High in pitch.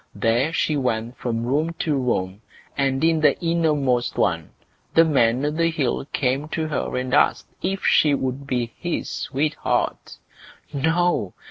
No: medium, 140 Hz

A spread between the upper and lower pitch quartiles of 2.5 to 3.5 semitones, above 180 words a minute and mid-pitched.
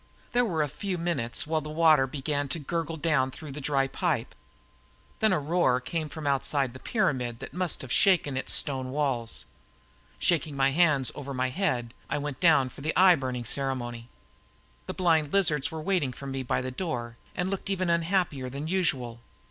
No: average, 4.3 semitones; average, 190 wpm; medium, 145 Hz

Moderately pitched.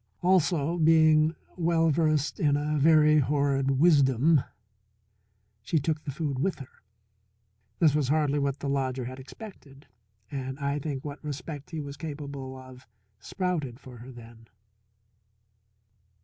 Yes: medium, 145 Hz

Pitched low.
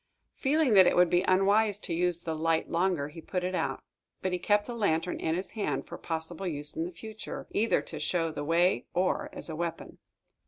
No: medium, 175 Hz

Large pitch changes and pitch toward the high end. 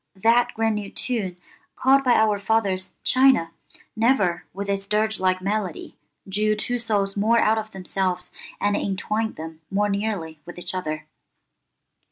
No: average, 3.0 semitones; high, 205 Hz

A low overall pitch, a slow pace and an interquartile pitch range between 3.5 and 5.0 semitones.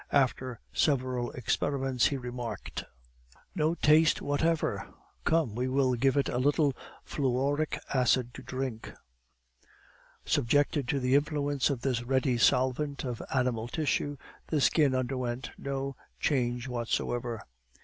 No: low, 130 Hz; slow, 120 wpm; narrow, 2.6 semitones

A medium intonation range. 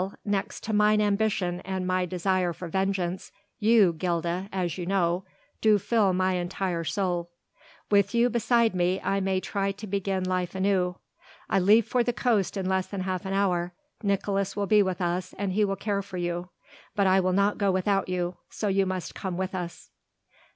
No: narrow, 1.9 semitones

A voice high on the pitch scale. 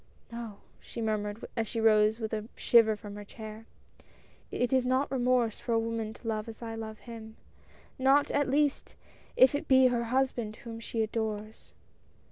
Yes: high, 225 Hz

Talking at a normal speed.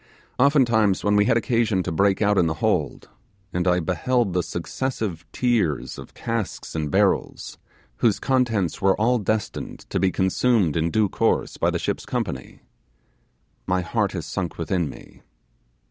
Yes: average, 160 wpm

